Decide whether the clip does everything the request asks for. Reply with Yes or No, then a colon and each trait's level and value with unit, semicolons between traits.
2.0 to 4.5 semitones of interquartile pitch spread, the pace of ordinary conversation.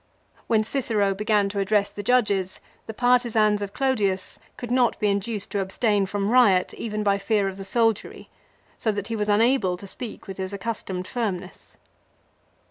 Yes: narrow, 2.6 semitones; average, 170 wpm